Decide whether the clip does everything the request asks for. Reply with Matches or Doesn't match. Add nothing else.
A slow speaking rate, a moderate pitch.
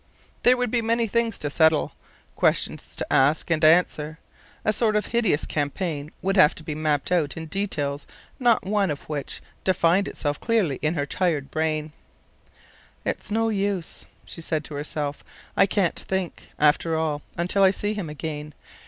Doesn't match